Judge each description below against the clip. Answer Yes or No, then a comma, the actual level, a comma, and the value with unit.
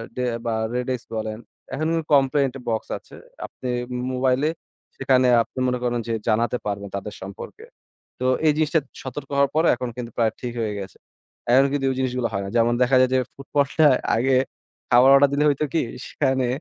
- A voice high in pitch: No, low, 130 Hz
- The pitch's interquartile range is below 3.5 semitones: Yes, average, 2.8 semitones